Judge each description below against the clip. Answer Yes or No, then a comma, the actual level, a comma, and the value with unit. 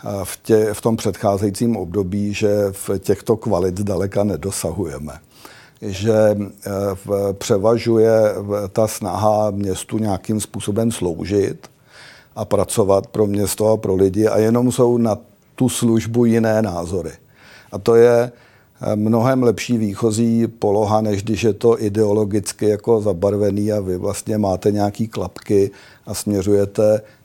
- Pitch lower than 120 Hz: Yes, low, 105 Hz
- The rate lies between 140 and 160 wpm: No, average, 130 wpm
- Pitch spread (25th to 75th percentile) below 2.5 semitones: Yes, narrow, 2.0 semitones